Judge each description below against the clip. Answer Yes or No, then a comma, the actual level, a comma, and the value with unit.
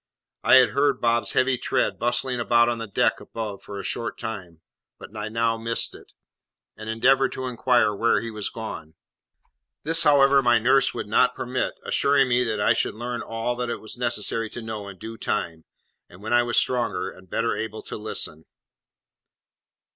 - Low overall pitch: Yes, low, 115 Hz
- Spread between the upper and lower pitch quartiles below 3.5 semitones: Yes, narrow, 2.4 semitones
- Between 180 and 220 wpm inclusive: Yes, average, 185 wpm